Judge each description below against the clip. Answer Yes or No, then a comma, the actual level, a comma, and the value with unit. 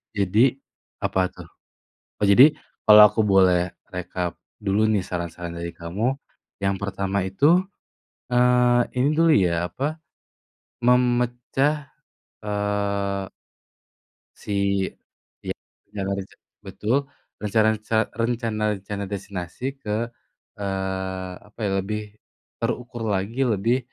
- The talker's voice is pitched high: No, low, 105 Hz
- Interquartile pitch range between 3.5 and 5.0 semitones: Yes, average, 4.1 semitones